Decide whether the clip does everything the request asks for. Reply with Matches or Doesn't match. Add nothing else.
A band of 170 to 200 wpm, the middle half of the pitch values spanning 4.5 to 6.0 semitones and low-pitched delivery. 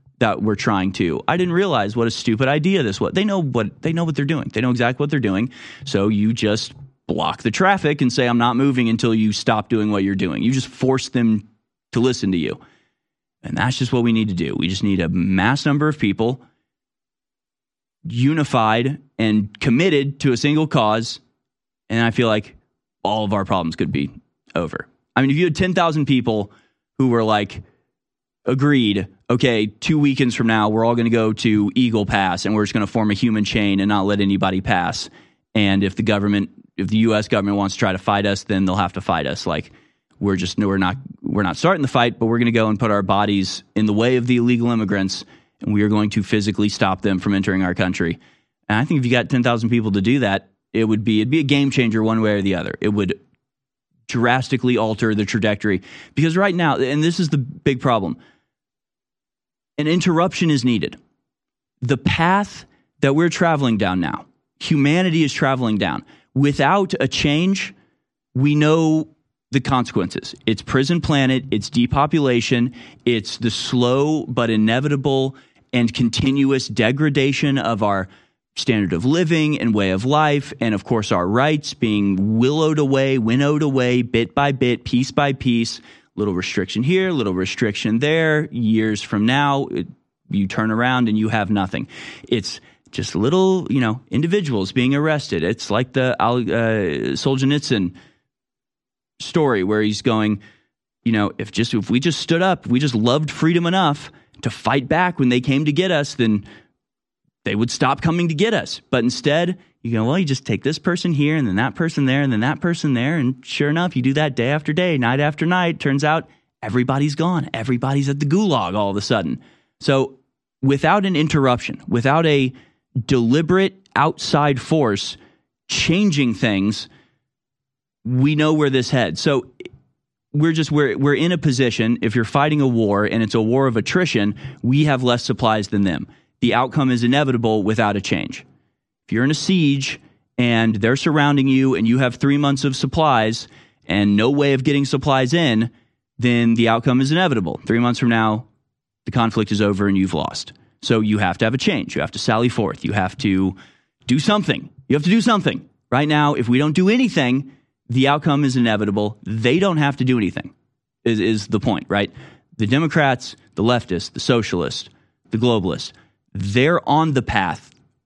Matches